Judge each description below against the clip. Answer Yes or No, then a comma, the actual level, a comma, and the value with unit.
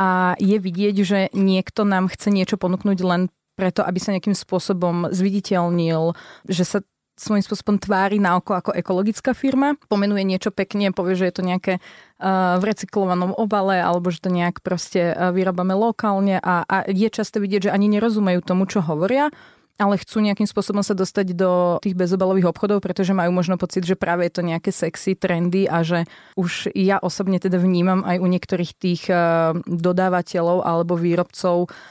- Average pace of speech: No, fast, 170 wpm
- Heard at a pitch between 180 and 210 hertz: Yes, medium, 185 Hz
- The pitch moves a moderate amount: No, narrow, 2.1 semitones